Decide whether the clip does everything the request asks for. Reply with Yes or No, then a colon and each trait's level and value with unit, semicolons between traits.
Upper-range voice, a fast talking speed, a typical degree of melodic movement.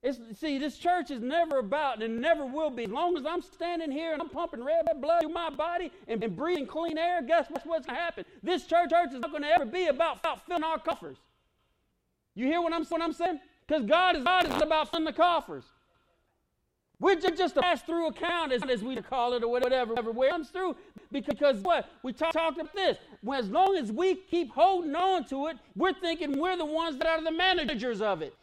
Yes: very high, 325 Hz; fast, 230 wpm; average, 3.5 semitones